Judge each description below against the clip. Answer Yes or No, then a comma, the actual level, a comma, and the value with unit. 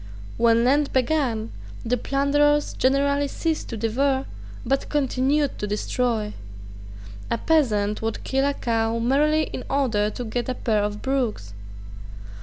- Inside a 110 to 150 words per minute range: Yes, slow, 135 wpm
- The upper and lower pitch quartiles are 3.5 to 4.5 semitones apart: Yes, average, 4.0 semitones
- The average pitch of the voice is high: Yes, very high, 255 Hz